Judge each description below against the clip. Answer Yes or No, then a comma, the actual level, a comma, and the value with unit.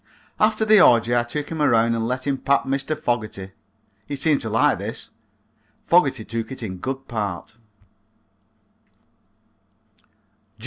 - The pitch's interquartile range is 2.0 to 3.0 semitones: No, average, 4.0 semitones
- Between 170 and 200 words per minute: No, slow, 135 wpm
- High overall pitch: No, low, 125 Hz